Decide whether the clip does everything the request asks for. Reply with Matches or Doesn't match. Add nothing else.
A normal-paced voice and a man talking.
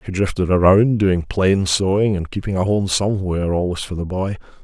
Matches